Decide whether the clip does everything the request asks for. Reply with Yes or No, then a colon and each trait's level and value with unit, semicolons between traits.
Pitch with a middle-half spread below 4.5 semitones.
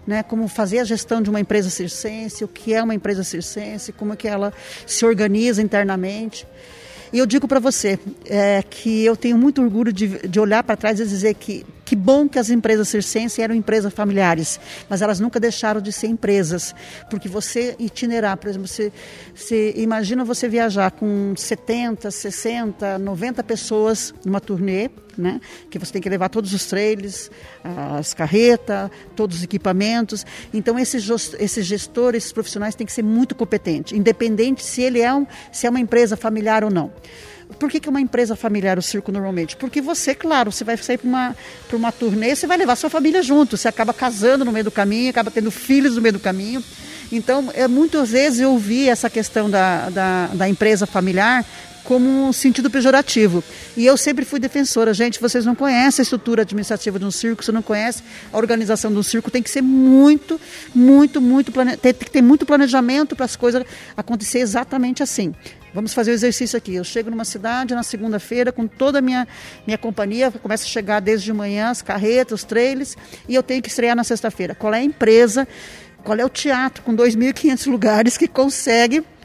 Yes: average, 3.2 semitones